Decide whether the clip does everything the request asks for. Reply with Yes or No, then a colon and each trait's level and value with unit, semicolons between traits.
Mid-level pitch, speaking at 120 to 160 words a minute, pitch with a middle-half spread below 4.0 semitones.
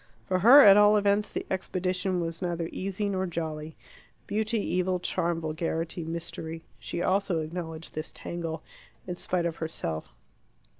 Yes: medium, 175 Hz; average, 145 wpm; average, 2.7 semitones